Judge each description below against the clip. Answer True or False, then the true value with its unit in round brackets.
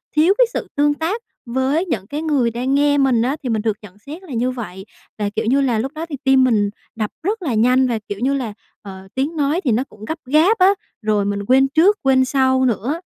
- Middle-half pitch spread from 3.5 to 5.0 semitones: True (4.6 semitones)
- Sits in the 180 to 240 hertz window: False (260 Hz)